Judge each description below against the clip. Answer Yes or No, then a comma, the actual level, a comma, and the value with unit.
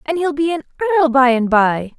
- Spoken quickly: Yes, fast, 240 wpm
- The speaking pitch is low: No, very high, 285 Hz